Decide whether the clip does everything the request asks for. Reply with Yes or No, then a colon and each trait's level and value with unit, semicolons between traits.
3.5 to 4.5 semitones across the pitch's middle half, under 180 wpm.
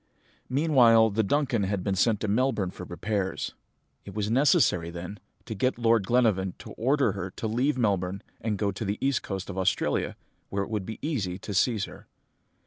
No: average, 3.8 semitones; average, 190 wpm